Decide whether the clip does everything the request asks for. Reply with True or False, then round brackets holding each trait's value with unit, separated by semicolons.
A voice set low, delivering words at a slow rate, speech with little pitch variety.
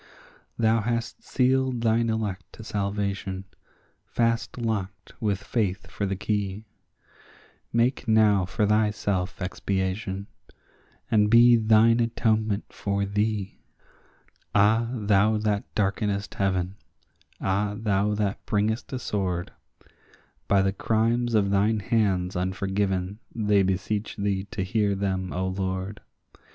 True (105 Hz; 115 wpm; 2.3 semitones)